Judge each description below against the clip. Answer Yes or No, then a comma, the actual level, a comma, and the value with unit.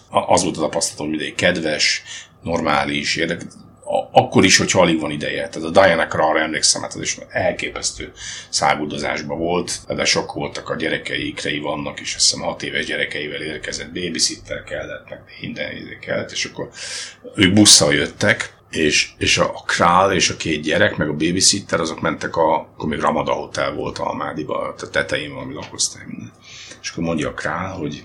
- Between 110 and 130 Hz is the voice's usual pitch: No, very low, 85 Hz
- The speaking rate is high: Yes, fast, 175 wpm